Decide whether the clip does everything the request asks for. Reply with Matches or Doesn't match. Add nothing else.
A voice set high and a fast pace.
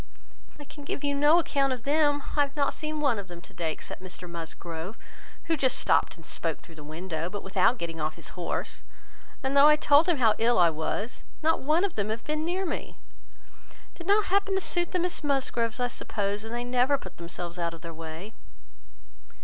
Matches